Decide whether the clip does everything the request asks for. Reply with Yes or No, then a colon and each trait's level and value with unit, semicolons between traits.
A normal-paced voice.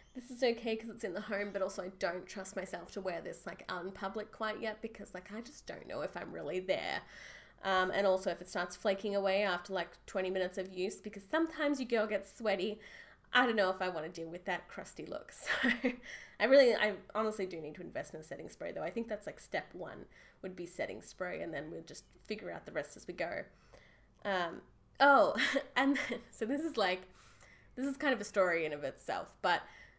No: fast, 235 wpm